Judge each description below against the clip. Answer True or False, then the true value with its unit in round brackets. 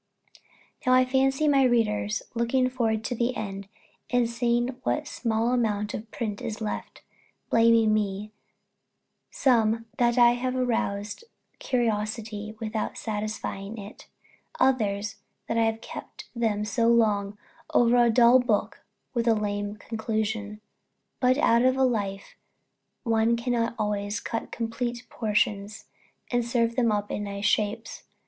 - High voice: True (225 Hz)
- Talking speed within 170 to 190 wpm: False (140 wpm)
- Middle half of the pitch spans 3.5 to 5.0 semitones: False (2.4 semitones)